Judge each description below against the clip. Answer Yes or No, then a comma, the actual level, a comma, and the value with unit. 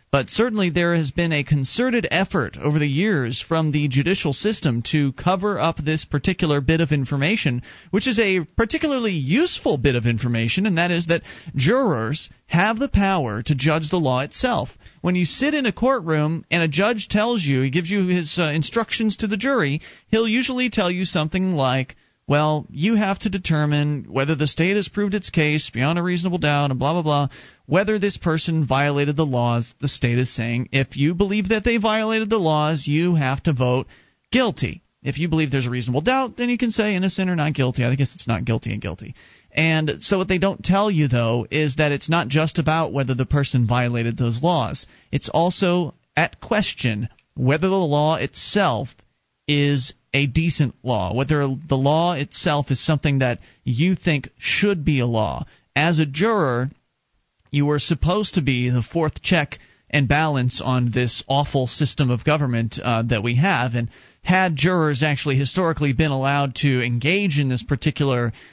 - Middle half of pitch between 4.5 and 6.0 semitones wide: Yes, average, 5.3 semitones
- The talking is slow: No, average, 190 wpm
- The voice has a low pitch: No, medium, 150 Hz